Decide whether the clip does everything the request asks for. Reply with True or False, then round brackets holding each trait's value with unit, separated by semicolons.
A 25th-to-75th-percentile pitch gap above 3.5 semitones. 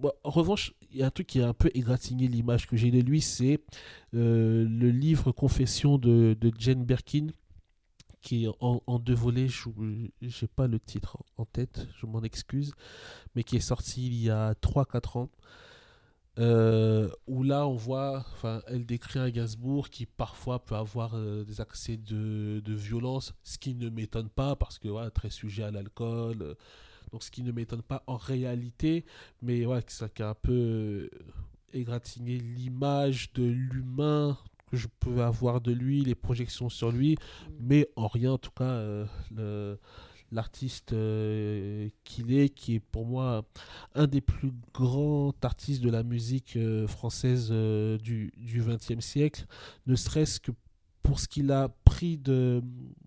False (2.9 semitones)